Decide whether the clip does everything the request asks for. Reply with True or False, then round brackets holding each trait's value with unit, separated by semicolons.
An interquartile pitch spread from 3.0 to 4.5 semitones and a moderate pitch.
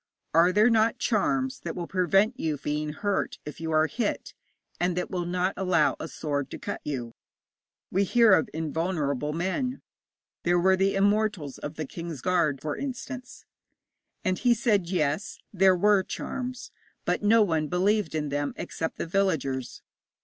False (4.9 semitones; 180 Hz)